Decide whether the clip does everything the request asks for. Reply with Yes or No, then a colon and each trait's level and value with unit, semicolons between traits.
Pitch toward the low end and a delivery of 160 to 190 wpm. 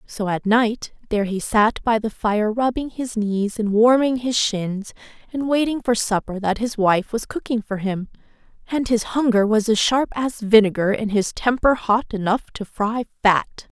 No: high, 220 Hz; average, 185 wpm